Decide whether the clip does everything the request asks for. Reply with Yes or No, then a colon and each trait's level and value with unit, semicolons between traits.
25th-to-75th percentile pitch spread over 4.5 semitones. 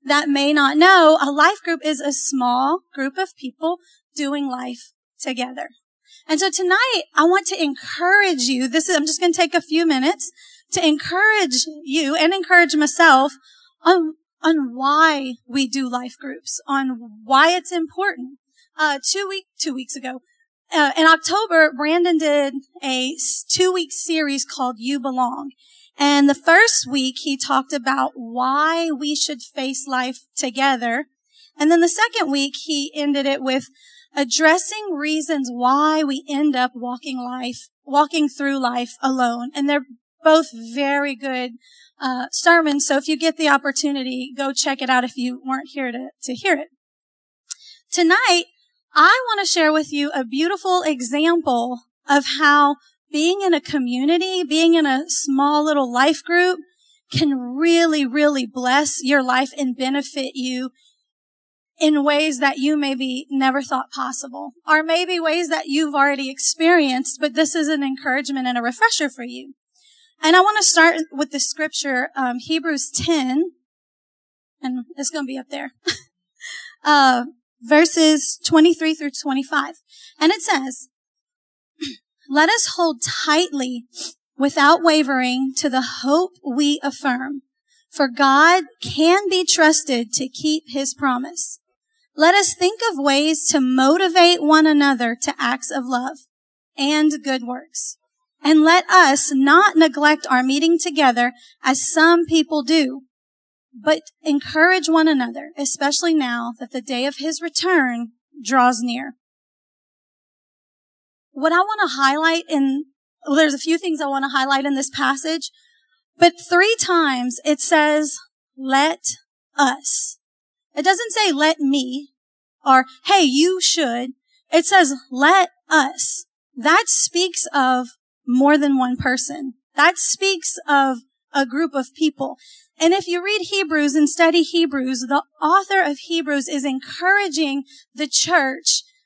No: average, 3.8 semitones